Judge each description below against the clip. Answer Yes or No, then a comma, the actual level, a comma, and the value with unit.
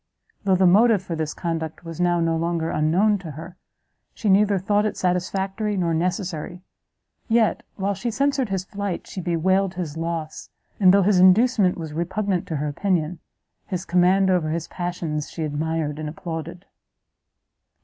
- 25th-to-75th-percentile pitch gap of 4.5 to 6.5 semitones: No, average, 3.0 semitones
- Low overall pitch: No, medium, 180 Hz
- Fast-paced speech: No, average, 160 wpm